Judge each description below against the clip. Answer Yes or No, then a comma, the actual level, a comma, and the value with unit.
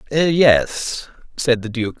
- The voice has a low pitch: Yes, low, 130 Hz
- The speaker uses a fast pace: No, slow, 120 wpm